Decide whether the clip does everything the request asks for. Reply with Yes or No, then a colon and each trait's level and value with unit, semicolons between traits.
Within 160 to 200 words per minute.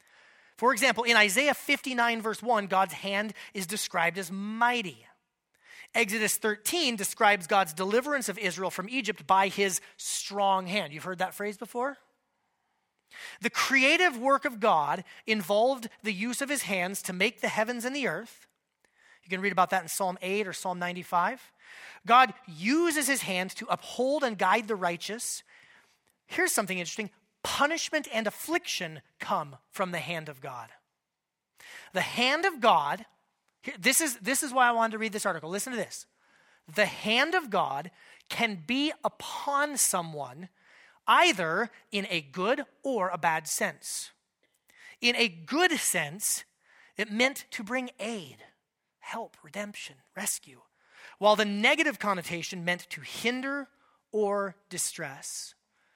No: average, 145 wpm